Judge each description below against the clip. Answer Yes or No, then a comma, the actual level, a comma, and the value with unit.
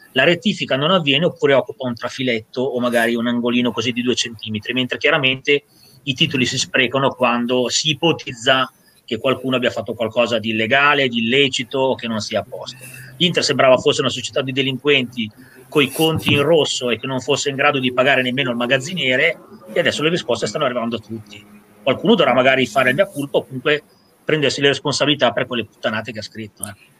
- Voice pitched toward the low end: Yes, low, 130 Hz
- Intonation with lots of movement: No, average, 2.8 semitones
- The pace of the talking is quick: Yes, fast, 200 wpm